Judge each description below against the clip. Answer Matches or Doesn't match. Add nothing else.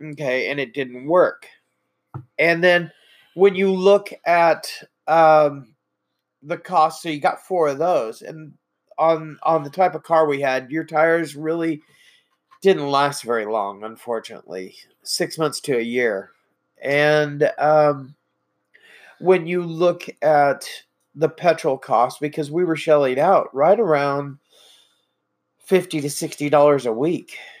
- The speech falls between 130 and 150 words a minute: Matches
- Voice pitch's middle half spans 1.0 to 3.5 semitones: Matches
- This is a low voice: Doesn't match